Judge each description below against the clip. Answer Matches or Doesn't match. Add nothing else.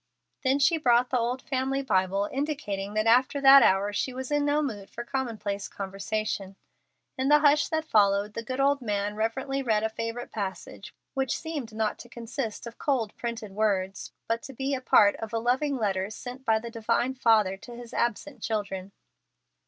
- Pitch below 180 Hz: Doesn't match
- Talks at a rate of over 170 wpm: Matches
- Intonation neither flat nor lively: Matches